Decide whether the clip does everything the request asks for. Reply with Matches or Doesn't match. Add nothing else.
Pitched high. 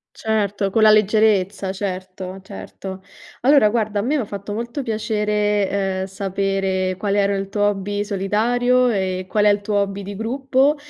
Matches